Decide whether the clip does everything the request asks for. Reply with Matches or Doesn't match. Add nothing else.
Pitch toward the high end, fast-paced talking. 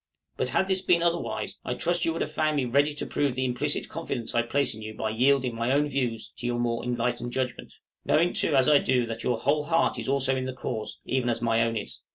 Doesn't match